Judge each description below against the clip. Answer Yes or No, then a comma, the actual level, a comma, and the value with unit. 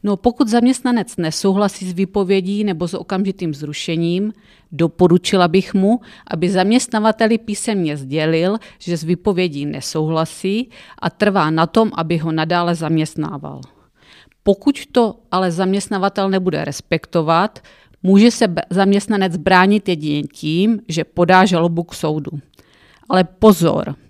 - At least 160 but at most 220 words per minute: No, average, 120 wpm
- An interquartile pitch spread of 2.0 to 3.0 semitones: No, average, 3.7 semitones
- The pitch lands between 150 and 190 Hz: Yes, medium, 185 Hz